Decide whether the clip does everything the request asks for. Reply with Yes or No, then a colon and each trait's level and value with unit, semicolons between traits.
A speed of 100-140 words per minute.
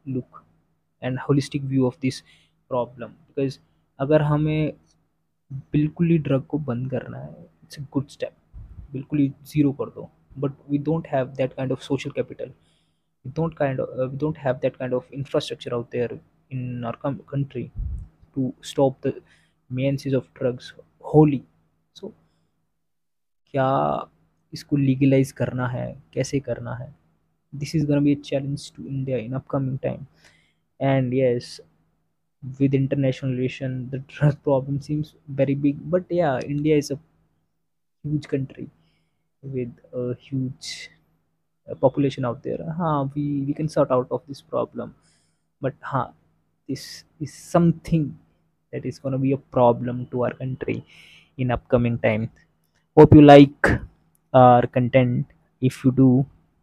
Yes: average, 130 wpm